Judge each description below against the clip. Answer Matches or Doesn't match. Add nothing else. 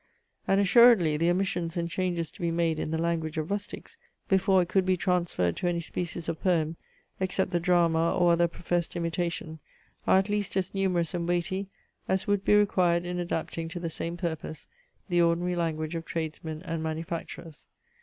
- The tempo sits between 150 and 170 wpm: Doesn't match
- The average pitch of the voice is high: Doesn't match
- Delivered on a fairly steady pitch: Matches